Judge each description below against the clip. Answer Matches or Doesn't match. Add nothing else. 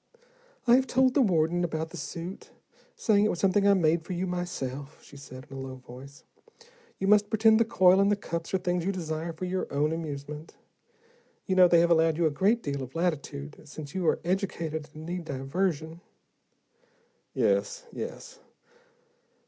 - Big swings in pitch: Doesn't match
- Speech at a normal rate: Matches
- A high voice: Doesn't match